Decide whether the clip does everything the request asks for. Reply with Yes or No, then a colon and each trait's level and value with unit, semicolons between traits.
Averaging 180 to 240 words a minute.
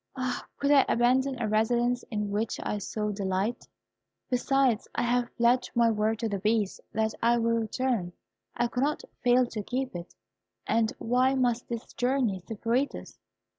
No: average, 165 wpm